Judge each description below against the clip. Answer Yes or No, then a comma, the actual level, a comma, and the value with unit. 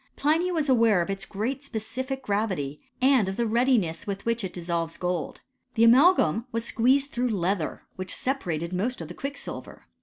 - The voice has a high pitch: Yes, high, 225 Hz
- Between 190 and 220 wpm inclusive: No, average, 175 wpm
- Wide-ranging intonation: Yes, wide, 6.2 semitones